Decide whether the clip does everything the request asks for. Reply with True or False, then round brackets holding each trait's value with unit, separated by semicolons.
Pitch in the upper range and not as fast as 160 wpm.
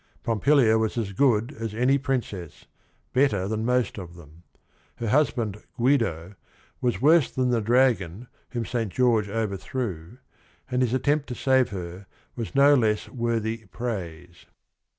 False (115 Hz; 140 wpm)